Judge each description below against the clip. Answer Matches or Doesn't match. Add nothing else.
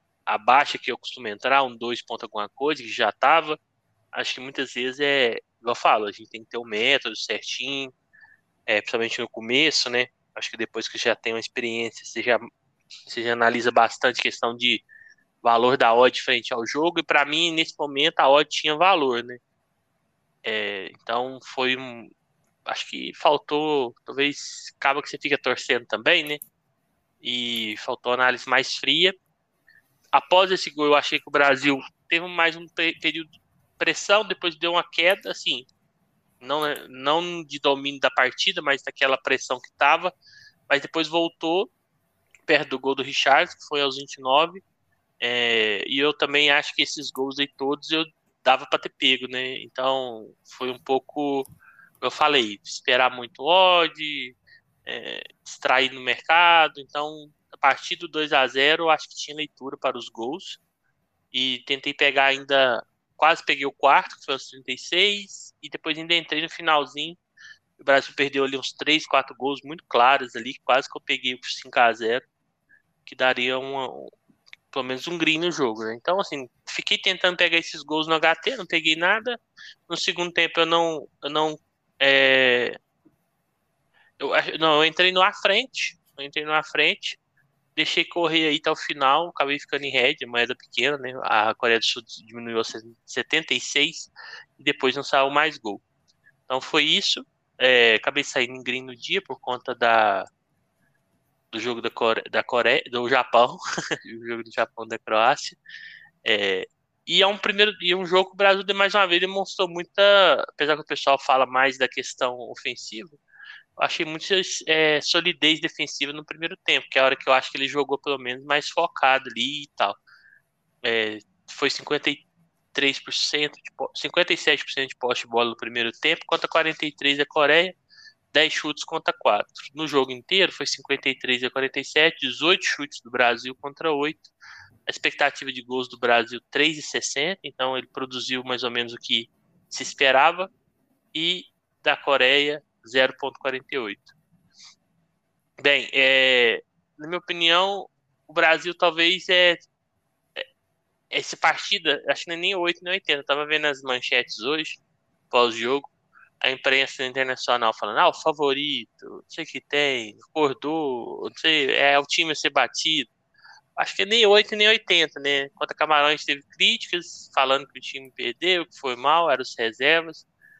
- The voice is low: Doesn't match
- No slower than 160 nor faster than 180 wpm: Matches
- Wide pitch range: Doesn't match